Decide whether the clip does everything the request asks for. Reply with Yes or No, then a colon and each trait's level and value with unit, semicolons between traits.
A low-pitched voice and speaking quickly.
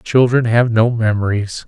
No: low, 115 Hz; average, 145 wpm